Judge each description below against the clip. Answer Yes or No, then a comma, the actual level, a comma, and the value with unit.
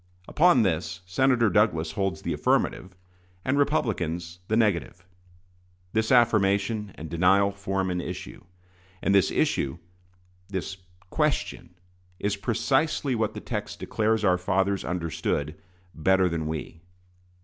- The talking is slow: Yes, slow, 120 wpm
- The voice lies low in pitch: Yes, very low, 95 Hz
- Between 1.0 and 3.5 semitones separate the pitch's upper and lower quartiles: No, average, 4.1 semitones